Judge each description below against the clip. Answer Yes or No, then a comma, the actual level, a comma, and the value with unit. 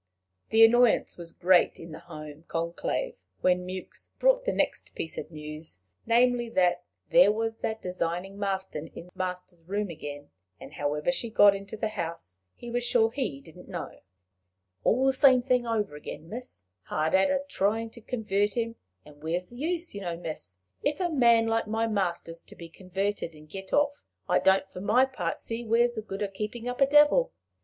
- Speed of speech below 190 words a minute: No, average, 195 wpm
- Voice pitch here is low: No, high, 205 Hz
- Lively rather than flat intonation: Yes, wide, 5.8 semitones